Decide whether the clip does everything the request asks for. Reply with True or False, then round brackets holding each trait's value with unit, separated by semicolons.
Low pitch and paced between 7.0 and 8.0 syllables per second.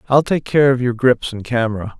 False (125 Hz; 5.5 syllables/s)